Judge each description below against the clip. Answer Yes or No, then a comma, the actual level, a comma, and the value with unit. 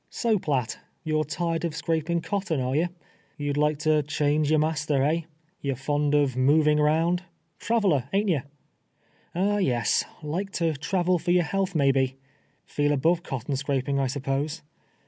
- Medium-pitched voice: Yes, medium, 150 Hz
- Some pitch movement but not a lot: Yes, average, 3.2 semitones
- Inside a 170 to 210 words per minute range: Yes, average, 180 wpm